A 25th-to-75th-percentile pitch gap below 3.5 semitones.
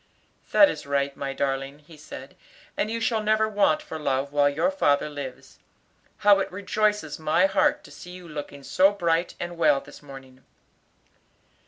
No: wide, 5.6 semitones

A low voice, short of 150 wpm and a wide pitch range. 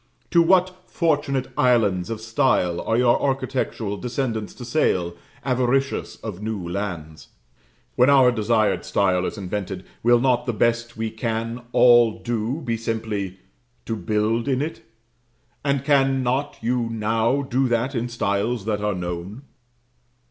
No: low, 115 Hz; average, 140 wpm; average, 3.6 semitones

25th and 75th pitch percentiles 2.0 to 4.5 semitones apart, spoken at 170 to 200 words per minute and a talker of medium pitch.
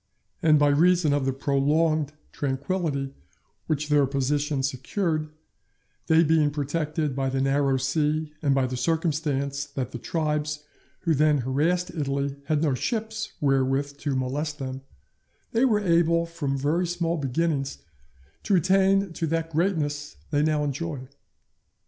No: average, 3.1 semitones; average, 140 wpm; medium, 150 Hz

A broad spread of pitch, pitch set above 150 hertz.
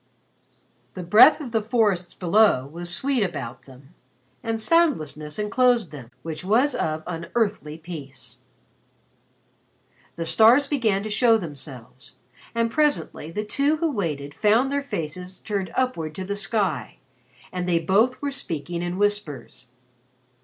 Yes: wide, 6.6 semitones; high, 190 Hz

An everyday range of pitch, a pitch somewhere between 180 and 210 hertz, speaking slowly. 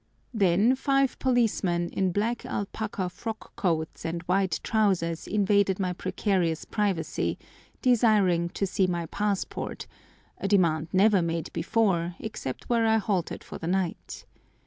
Yes: average, 3.9 semitones; high, 190 Hz; slow, 125 wpm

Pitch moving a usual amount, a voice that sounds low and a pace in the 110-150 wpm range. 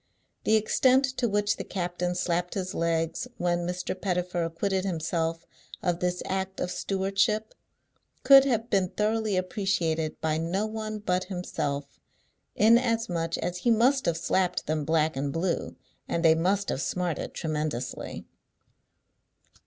No: average, 3.8 semitones; medium, 180 Hz; slow, 135 wpm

